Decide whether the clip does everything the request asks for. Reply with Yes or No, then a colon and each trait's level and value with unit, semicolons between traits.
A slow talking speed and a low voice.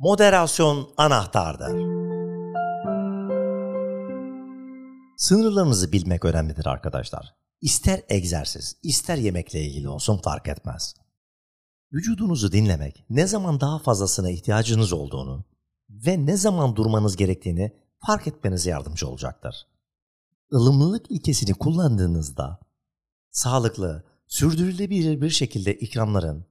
Yes: slow, 90 wpm; low, 110 Hz